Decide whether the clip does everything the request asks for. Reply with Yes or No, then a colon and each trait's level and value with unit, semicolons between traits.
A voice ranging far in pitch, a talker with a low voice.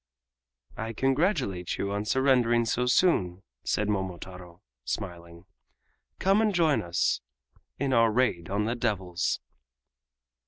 Yes: wide, 6.2 semitones; low, 105 Hz